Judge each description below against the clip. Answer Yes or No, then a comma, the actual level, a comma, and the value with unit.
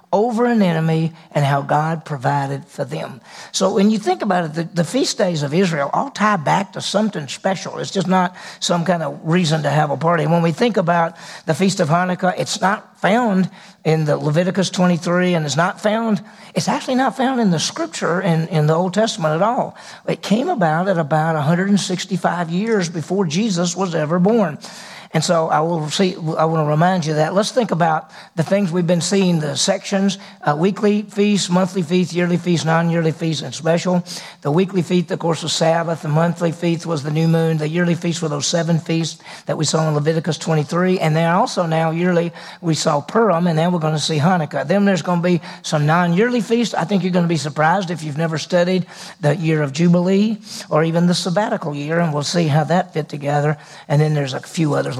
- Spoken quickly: Yes, fast, 220 wpm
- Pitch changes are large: No, average, 3.1 semitones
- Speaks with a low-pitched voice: No, medium, 175 Hz